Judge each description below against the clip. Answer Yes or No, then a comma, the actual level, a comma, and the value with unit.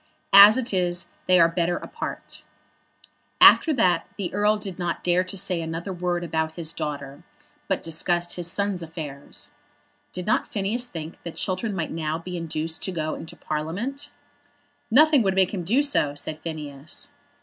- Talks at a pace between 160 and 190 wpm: Yes, average, 165 wpm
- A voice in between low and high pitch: Yes, medium, 175 Hz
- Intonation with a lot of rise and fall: No, average, 3.5 semitones